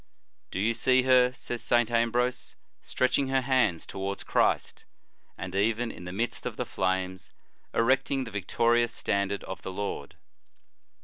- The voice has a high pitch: No, low, 115 Hz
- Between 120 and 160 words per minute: Yes, average, 150 wpm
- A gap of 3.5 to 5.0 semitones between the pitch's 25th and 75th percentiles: Yes, average, 4.4 semitones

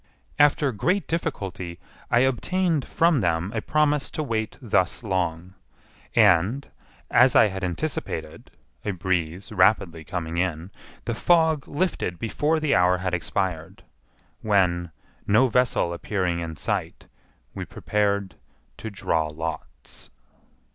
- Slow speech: Yes, slow, 120 wpm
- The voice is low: Yes, low, 100 Hz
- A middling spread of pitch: No, wide, 7.3 semitones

